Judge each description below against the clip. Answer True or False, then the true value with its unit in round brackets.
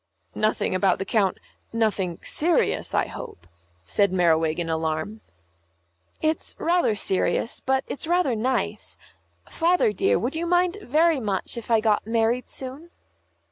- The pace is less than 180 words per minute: True (140 wpm)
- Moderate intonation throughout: False (8.4 semitones)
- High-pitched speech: True (225 Hz)